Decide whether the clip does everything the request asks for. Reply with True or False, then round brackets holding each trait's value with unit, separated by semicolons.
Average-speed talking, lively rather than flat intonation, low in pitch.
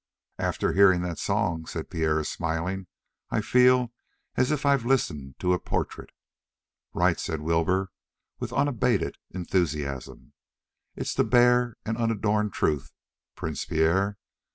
False (125 wpm; 6.2 semitones; 95 Hz)